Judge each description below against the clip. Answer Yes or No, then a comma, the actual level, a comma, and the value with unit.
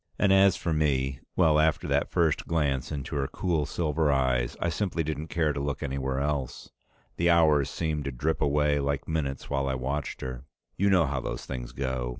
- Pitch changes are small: No, average, 3.0 semitones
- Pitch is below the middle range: Yes, very low, 75 Hz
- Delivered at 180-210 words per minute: Yes, average, 195 wpm